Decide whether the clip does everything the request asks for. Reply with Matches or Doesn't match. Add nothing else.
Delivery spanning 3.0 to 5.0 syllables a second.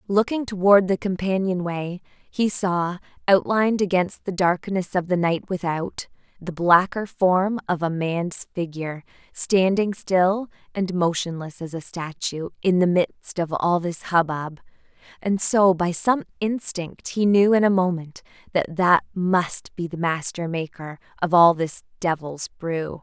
Matches